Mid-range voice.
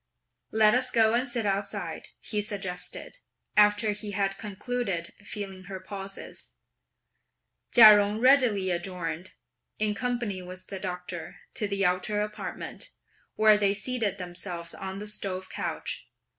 No: high, 200 Hz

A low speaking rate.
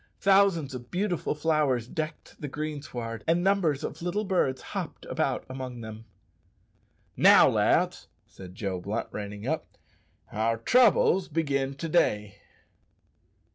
Yes: slow, 125 wpm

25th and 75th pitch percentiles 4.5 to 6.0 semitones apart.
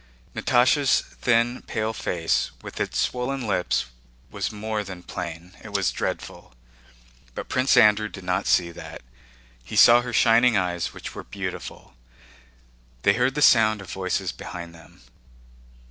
Yes: average, 5.1 semitones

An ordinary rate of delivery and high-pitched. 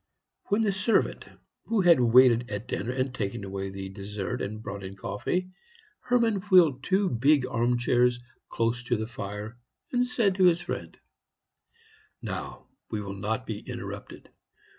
No: average, 155 wpm; low, 120 Hz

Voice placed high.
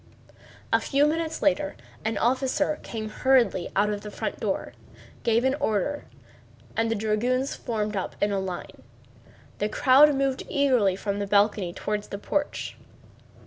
Yes: high, 225 Hz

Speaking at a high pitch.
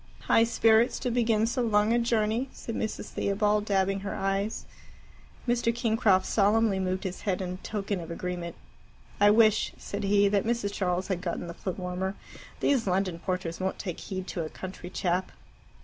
Yes: high, 200 Hz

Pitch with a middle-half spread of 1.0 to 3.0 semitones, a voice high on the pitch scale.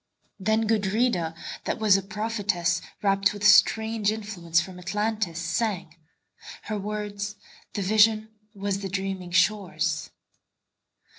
Yes: narrow, 2.6 semitones; high, 200 Hz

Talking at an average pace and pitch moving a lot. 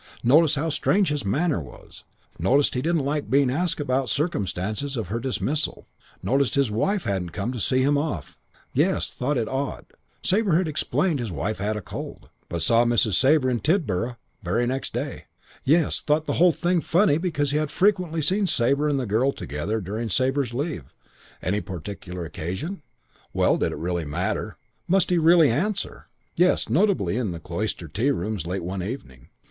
Yes: average, 175 wpm; wide, 7.2 semitones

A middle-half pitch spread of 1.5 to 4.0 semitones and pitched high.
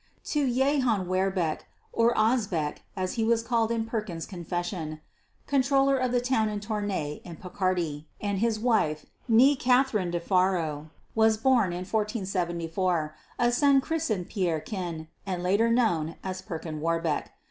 No: average, 5.2 semitones; high, 200 Hz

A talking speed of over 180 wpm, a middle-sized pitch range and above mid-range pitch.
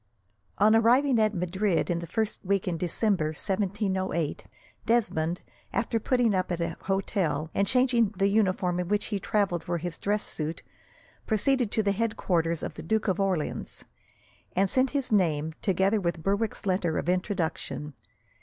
No: average, 165 wpm; average, 3.9 semitones; high, 195 Hz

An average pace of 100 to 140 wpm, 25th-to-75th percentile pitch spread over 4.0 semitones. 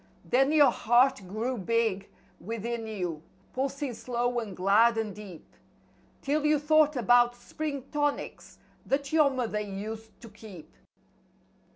Yes: slow, 135 wpm; average, 4.5 semitones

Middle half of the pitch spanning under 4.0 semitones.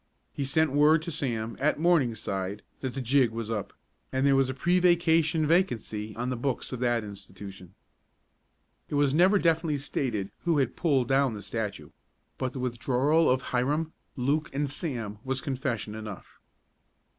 No: average, 5.0 semitones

